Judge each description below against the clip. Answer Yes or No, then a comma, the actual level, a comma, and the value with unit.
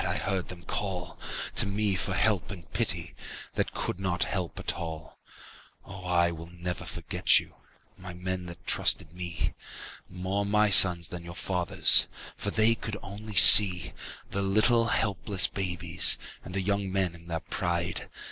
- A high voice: No, very low, 95 Hz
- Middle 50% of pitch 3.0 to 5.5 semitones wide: No, narrow, 2.4 semitones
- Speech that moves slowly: No, average, 160 wpm